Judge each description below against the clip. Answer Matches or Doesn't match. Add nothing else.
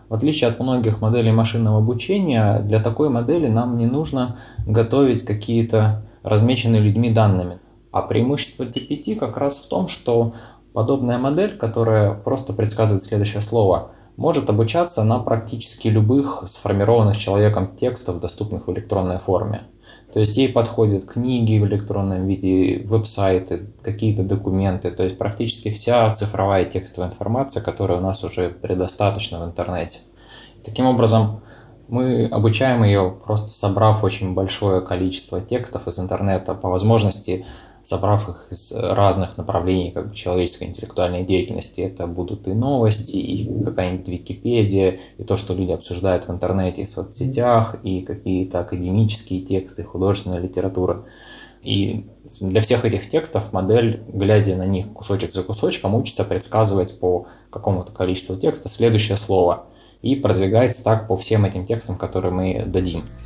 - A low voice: Matches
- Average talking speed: Matches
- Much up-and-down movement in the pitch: Doesn't match